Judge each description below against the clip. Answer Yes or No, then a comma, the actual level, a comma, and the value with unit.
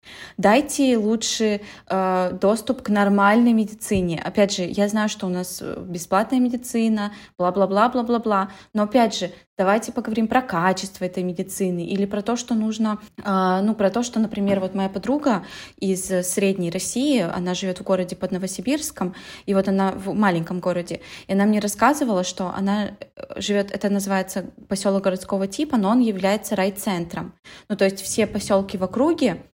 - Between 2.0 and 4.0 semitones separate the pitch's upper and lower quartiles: Yes, average, 2.7 semitones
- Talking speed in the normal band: No, fast, 170 wpm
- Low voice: No, high, 200 Hz